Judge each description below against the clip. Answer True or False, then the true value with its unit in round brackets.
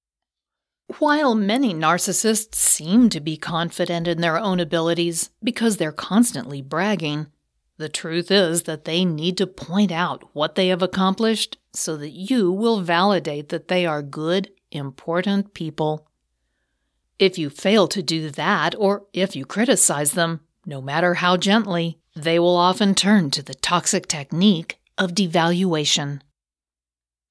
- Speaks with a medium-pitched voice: True (175 Hz)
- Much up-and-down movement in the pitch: False (3.9 semitones)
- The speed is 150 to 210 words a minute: False (140 wpm)